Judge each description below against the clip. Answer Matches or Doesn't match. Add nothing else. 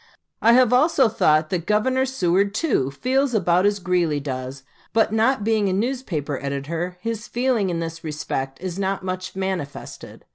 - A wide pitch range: Matches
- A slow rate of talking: Doesn't match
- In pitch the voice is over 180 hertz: Matches